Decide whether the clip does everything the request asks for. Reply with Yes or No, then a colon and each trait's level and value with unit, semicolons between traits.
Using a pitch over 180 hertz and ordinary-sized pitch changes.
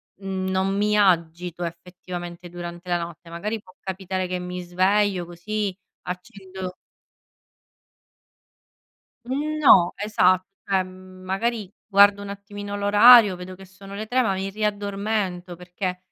No: high, 190 Hz; narrow, 2.2 semitones